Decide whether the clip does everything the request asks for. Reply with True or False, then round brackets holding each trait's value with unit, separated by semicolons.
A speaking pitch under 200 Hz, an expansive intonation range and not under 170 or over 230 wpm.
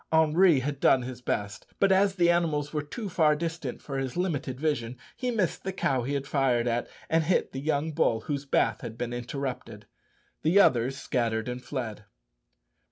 False (140 Hz; 4.8 semitones; 180 wpm)